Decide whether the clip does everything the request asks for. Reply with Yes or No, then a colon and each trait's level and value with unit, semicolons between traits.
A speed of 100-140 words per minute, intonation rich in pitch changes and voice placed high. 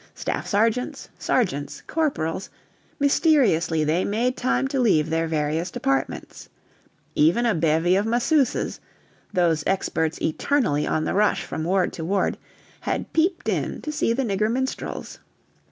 Yes: slow, 135 wpm; wide, 7.6 semitones; high, 195 Hz